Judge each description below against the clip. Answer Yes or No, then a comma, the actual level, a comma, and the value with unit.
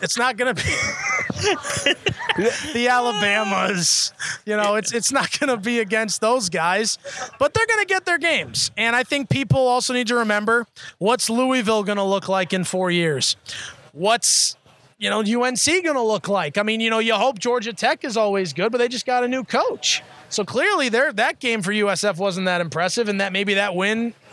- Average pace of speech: Yes, average, 190 wpm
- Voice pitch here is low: No, high, 225 Hz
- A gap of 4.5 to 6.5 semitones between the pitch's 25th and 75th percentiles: No, average, 4.0 semitones